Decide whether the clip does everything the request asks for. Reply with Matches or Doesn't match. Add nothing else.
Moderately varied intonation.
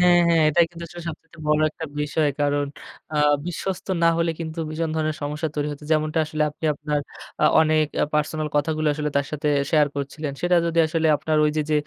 Doesn't match